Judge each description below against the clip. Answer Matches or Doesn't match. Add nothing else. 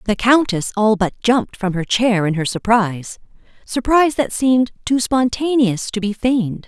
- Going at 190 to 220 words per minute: Doesn't match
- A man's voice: Doesn't match